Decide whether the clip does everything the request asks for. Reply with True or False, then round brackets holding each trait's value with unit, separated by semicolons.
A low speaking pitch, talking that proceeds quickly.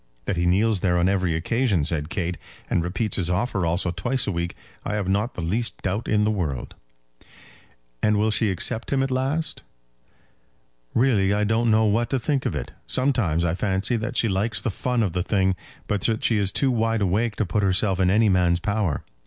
True (105 Hz; 210 wpm)